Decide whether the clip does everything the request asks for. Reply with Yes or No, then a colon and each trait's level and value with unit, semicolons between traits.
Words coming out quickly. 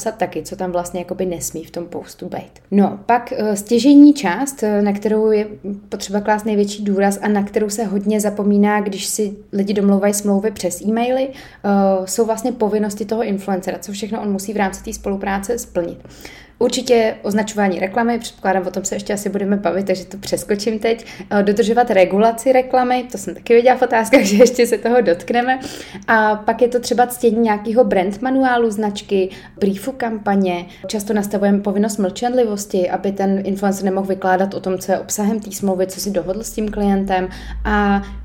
Yes: fast, 175 wpm